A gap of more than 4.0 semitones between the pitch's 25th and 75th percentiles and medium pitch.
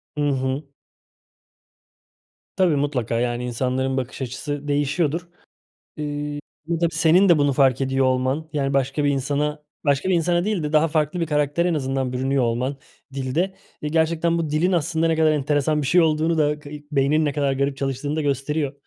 No: average, 2.8 semitones; medium, 145 Hz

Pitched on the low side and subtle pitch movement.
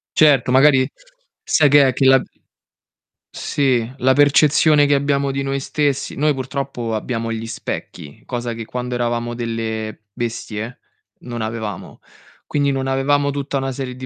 No: low, 130 Hz; average, 3.1 semitones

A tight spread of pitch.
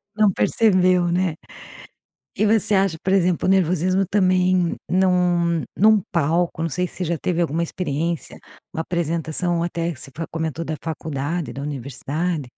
Yes: narrow, 2.3 semitones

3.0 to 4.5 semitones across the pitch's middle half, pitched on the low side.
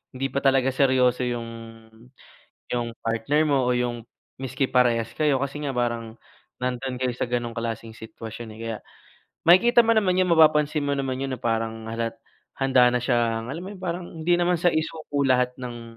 Yes: average, 3.5 semitones; low, 125 Hz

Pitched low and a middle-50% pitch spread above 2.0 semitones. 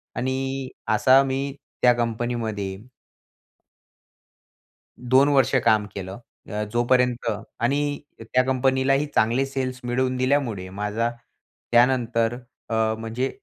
Yes: low, 125 Hz; narrow, 2.6 semitones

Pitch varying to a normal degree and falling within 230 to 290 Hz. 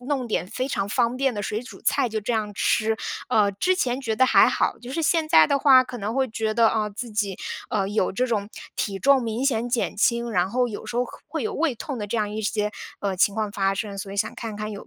No: average, 3.4 semitones; high, 220 Hz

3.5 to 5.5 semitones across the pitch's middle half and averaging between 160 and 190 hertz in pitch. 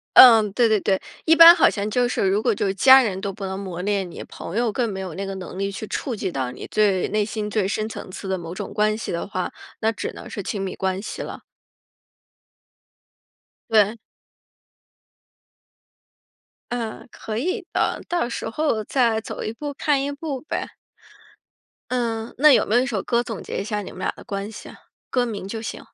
No: average, 3.8 semitones; high, 215 Hz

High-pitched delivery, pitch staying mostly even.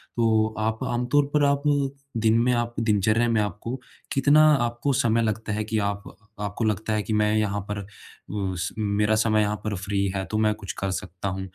No: low, 110 Hz; narrow, 2.2 semitones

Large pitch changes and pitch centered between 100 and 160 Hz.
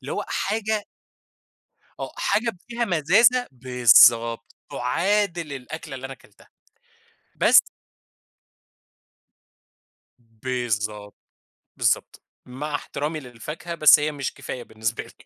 Yes: wide, 6.4 semitones; medium, 140 Hz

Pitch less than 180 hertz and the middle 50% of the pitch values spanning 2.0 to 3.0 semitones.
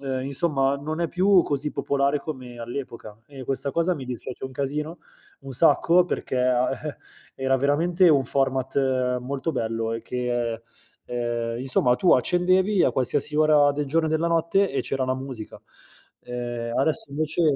No: low, 135 Hz; average, 3.7 semitones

